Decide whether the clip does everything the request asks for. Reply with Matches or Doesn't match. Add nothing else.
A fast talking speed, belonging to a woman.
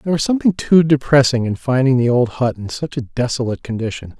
Doesn't match